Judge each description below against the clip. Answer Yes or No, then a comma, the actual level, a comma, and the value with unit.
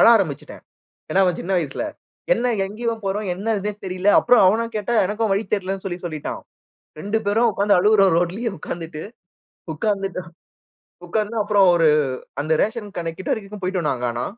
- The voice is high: Yes, high, 195 Hz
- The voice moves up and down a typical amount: Yes, average, 3.3 semitones